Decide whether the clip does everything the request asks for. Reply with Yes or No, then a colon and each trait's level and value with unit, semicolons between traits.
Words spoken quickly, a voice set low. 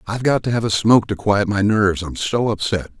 Yes: fast, 260 wpm; low, 105 Hz